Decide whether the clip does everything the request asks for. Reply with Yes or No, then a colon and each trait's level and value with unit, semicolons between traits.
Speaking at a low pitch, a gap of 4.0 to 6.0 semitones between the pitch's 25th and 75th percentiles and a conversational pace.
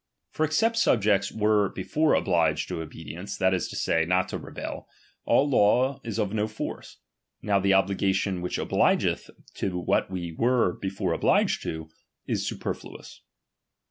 No: low, 100 Hz; average, 3.3 semitones; average, 160 wpm